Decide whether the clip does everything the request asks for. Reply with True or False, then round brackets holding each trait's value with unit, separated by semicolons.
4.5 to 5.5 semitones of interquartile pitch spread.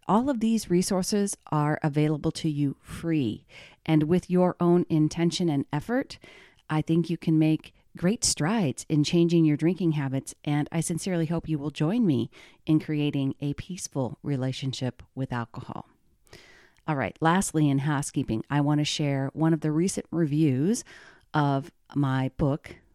False (3.1 semitones)